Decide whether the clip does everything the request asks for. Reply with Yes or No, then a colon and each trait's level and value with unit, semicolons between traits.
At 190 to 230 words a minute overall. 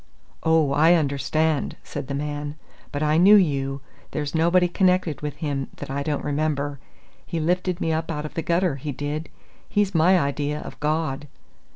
No: average, 175 wpm